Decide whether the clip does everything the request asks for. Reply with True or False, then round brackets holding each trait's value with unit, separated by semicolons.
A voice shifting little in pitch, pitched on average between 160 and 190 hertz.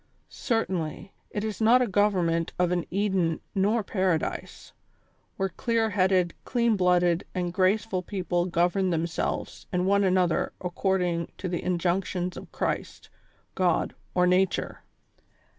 True (2.2 semitones; 185 Hz)